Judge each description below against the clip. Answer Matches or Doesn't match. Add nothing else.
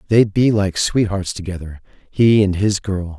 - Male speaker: Matches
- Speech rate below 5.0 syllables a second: Matches